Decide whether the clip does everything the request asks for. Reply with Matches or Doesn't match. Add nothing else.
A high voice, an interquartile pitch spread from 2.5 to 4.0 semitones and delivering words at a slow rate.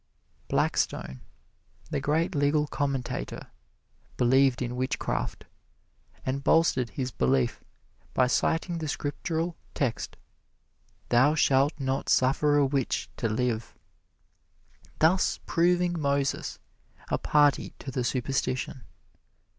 Doesn't match